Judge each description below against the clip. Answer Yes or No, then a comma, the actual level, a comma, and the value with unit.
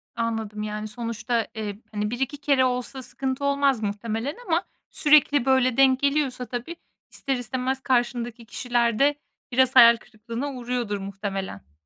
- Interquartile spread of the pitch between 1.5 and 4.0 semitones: Yes, average, 3.3 semitones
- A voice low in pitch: No, high, 245 Hz